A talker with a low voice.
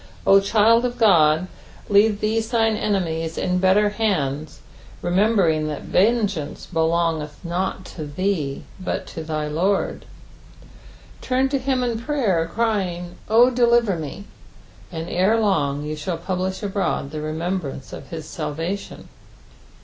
No: medium, 185 Hz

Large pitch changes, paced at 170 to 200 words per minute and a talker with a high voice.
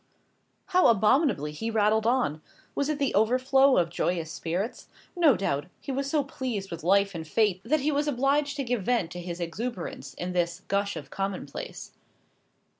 Yes: wide, 7.4 semitones; average, 175 wpm; high, 215 Hz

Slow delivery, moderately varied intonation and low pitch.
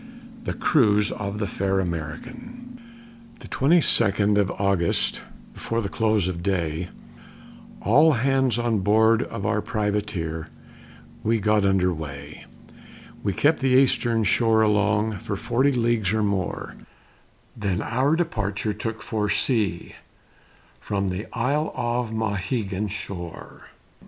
Yes: slow, 125 wpm; average, 3.4 semitones; low, 105 Hz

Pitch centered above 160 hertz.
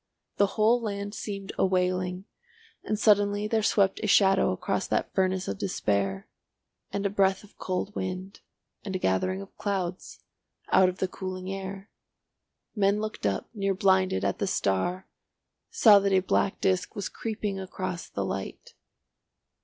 Yes: high, 190 Hz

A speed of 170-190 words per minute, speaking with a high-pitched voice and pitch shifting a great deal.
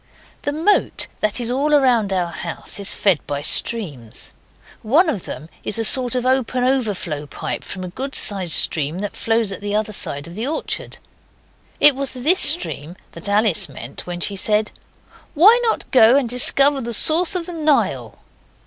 Yes: average, 180 wpm; high, 225 Hz; wide, 6.8 semitones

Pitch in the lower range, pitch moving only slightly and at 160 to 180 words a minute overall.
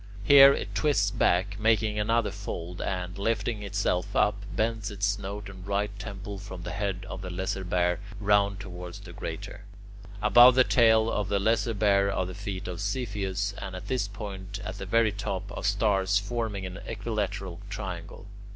Yes: low, 100 Hz; narrow, 2.1 semitones; average, 175 wpm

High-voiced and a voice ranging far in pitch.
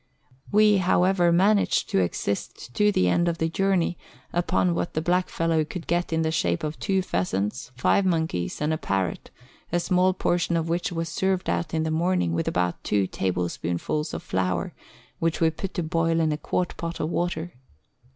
No: medium, 165 Hz; wide, 6.4 semitones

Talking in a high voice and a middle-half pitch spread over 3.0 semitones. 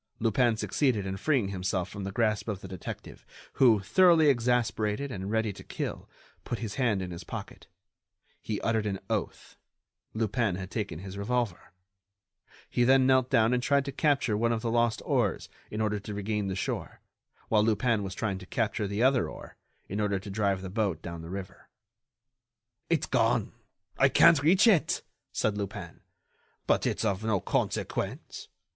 No: low, 110 Hz; average, 3.8 semitones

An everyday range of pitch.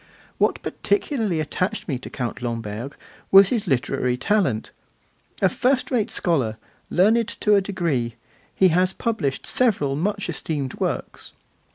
No: wide, 8.0 semitones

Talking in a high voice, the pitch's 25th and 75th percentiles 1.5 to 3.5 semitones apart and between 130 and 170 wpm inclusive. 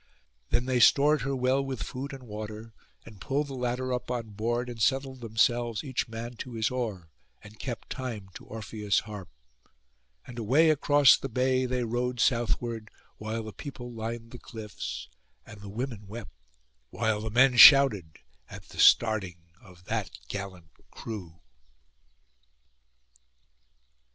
No: low, 115 Hz; average, 3.1 semitones; average, 145 wpm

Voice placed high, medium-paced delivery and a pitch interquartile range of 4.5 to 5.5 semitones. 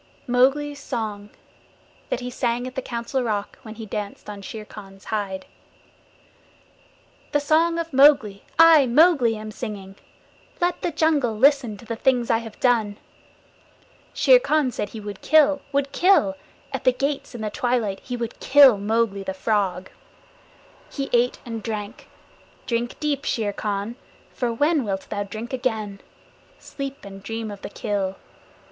Yes: high, 235 Hz; average, 155 wpm; average, 4.8 semitones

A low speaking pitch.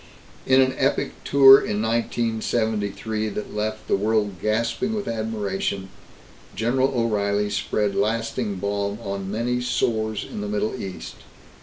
Yes: low, 110 Hz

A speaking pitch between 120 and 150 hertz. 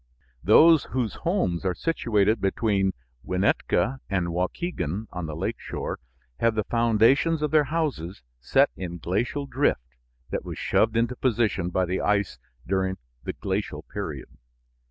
No: low, 105 Hz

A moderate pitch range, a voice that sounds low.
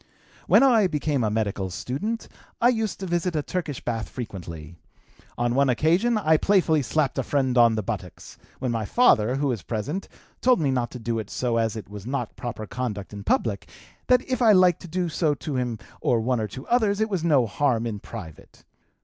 No: wide, 7.6 semitones; low, 130 Hz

